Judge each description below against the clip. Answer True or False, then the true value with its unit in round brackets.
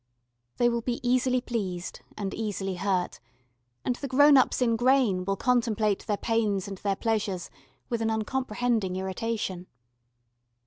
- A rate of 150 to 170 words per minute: False (140 wpm)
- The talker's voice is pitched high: True (220 Hz)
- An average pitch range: True (3.9 semitones)